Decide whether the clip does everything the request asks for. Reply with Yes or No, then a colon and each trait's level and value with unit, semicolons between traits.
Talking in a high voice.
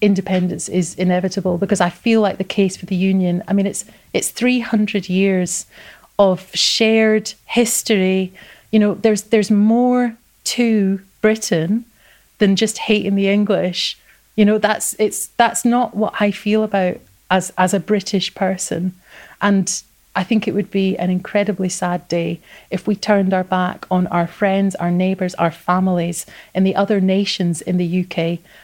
Yes: high, 195 Hz